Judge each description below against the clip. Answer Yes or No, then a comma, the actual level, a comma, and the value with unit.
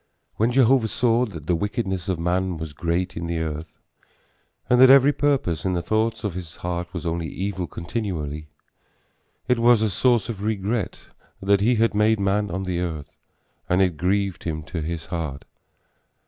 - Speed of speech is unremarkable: Yes, average, 175 wpm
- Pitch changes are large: No, average, 4.7 semitones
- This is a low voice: Yes, very low, 95 Hz